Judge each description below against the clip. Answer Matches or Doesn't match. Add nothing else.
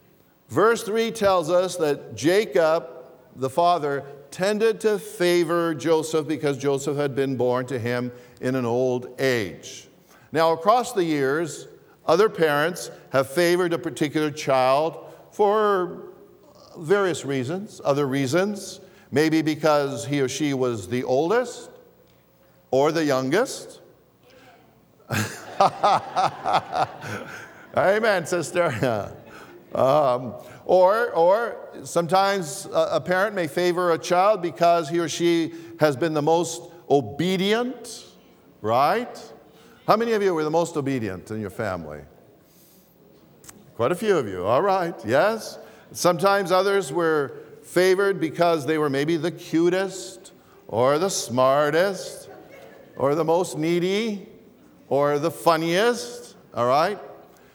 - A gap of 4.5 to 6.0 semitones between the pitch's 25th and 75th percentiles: Matches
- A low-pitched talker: Doesn't match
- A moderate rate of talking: Doesn't match